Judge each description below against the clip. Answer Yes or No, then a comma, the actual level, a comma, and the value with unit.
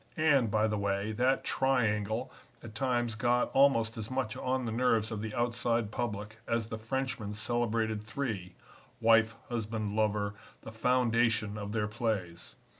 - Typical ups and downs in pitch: No, narrow, 2.2 semitones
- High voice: No, low, 115 Hz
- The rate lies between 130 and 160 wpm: Yes, average, 150 wpm